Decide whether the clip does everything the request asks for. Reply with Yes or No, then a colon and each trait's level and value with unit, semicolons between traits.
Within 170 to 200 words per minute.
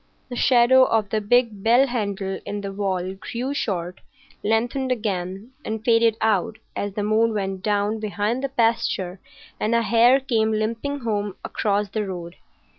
No: average, 160 wpm